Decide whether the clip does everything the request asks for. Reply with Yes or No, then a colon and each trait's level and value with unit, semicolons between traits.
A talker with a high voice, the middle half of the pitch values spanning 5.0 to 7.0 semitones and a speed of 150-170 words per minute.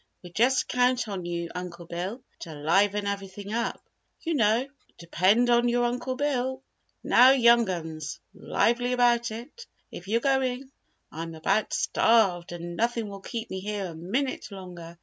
Yes: high, 215 Hz; wide, 5.5 semitones; average, 155 wpm